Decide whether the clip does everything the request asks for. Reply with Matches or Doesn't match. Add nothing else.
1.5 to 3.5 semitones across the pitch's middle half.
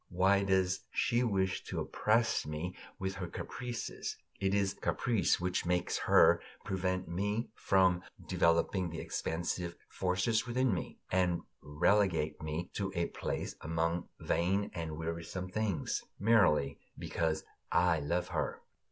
Matches